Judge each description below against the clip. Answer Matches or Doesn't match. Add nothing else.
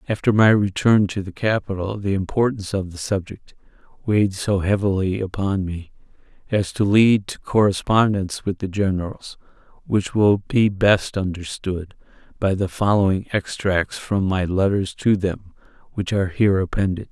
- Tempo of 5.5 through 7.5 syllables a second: Doesn't match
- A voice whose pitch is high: Doesn't match